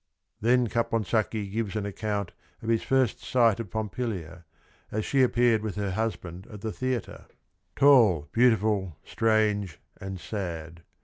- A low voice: Yes, low, 110 Hz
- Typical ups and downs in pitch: Yes, average, 3.1 semitones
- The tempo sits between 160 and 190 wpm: No, average, 145 wpm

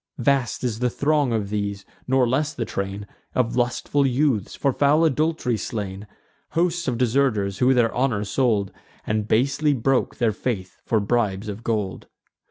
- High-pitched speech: No, low, 120 Hz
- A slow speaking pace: No, average, 160 wpm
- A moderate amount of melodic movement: Yes, average, 4.5 semitones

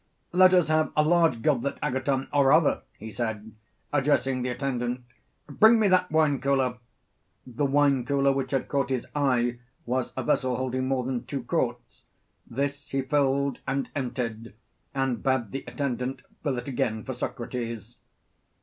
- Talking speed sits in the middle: Yes, average, 160 wpm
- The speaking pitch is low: Yes, low, 130 Hz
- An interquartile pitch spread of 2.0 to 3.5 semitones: Yes, narrow, 2.5 semitones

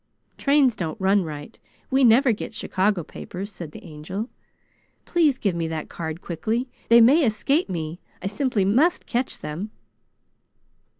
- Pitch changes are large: Yes, wide, 6.8 semitones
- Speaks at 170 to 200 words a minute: No, average, 145 wpm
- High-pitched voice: Yes, high, 205 Hz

